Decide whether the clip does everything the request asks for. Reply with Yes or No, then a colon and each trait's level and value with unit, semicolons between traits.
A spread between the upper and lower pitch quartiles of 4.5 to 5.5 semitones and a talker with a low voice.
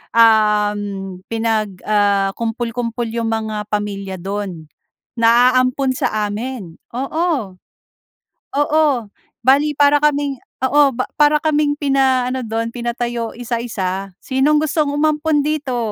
No: average, 5.0 semitones; high, 235 Hz